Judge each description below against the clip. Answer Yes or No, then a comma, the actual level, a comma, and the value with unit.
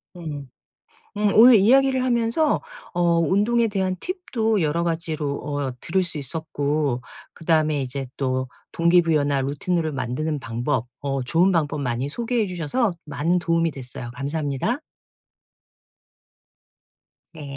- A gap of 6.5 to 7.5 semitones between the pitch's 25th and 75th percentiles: No, average, 5.3 semitones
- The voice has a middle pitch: Yes, medium, 160 Hz